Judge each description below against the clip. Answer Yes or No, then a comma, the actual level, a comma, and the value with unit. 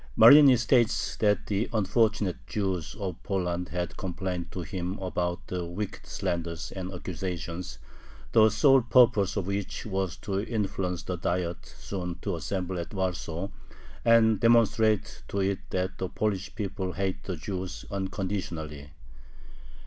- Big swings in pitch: No, average, 3.0 semitones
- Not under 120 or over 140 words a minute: Yes, slow, 135 wpm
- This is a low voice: Yes, very low, 95 Hz